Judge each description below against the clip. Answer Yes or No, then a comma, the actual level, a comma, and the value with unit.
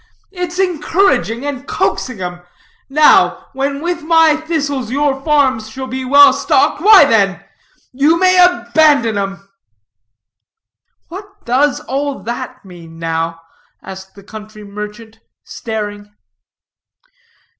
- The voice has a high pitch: Yes, very high, 260 Hz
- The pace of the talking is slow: Yes, slow, 115 wpm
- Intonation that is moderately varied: No, wide, 6.4 semitones